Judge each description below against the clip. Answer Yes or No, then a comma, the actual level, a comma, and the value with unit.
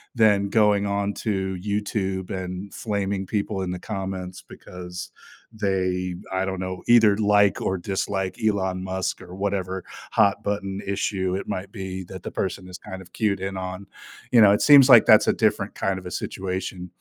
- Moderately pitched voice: No, very low, 95 Hz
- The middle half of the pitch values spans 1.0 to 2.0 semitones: Yes, narrow, 1.5 semitones